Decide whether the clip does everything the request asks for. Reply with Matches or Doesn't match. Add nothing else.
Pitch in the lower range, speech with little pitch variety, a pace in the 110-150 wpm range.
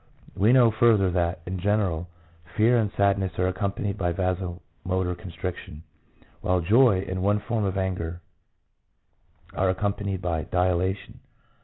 Matches